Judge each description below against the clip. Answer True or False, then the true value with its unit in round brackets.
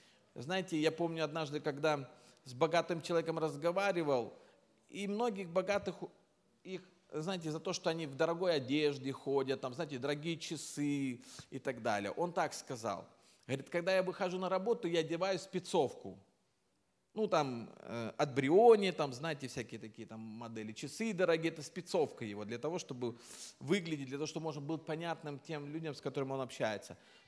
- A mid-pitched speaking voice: True (155 Hz)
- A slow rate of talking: False (160 wpm)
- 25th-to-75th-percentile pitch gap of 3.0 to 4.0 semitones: False (4.4 semitones)